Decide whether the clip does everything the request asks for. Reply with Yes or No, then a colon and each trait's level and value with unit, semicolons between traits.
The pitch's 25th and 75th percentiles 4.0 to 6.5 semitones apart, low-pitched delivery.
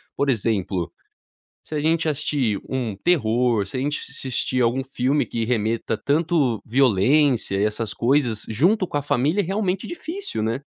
Yes: average, 5.1 semitones; low, 130 Hz